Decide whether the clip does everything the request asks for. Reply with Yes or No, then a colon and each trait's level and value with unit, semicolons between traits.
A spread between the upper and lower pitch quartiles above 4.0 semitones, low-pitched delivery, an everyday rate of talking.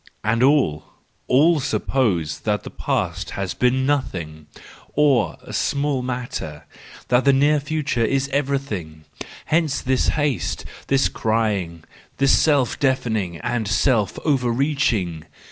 No: average, 5.3 semitones; low, 125 Hz; slow, 120 wpm